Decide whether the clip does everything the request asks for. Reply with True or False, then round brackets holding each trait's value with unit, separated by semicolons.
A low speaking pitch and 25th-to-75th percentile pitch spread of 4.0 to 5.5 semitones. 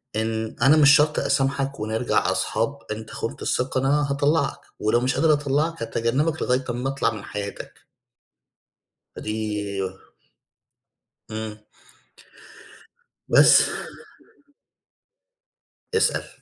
True (130 Hz; 4.6 semitones)